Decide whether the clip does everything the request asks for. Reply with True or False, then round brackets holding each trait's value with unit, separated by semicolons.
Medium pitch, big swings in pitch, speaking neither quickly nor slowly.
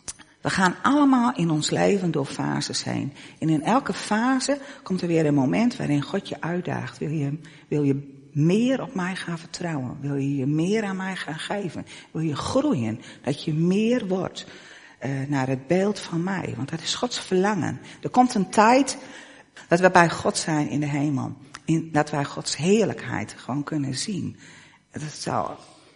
True (165 Hz; 5.7 semitones; 185 wpm)